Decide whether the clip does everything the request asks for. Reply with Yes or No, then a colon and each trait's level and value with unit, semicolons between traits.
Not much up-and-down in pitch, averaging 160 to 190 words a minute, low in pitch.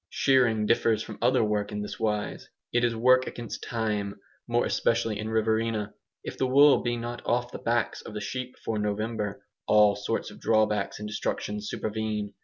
Yes: narrow, 2.1 semitones; average, 185 wpm; low, 110 Hz